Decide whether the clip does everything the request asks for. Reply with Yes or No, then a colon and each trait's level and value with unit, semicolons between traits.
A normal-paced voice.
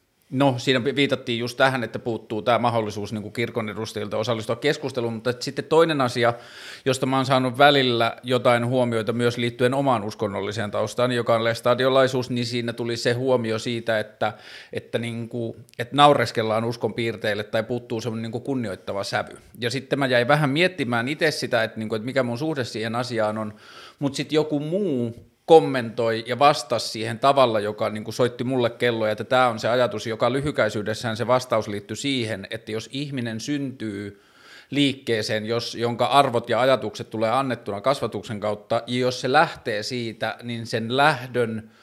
No: fast, 170 wpm